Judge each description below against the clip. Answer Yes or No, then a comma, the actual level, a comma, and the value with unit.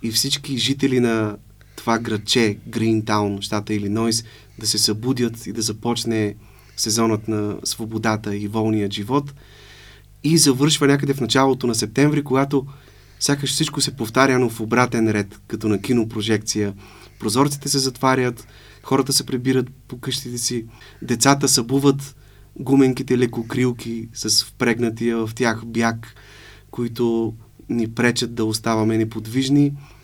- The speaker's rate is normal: Yes, average, 130 wpm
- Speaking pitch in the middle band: No, low, 115 Hz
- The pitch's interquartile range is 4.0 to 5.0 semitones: No, average, 3.4 semitones